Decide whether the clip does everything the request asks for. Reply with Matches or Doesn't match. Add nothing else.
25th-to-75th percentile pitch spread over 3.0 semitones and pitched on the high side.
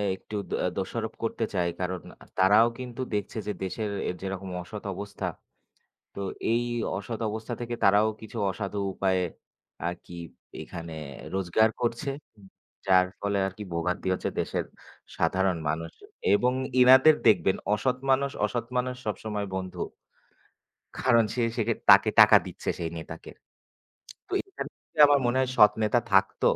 Doesn't match